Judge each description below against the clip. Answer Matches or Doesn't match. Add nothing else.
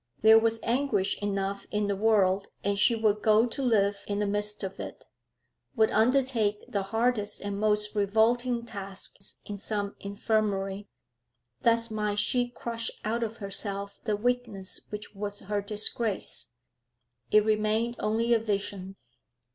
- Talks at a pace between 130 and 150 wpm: Matches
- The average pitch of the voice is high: Matches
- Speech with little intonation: Matches